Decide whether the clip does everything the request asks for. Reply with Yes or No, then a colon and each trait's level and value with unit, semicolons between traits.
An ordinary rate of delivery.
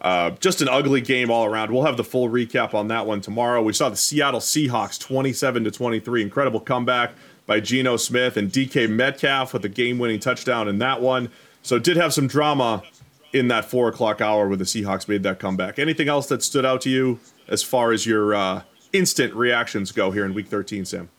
No: fast, 215 wpm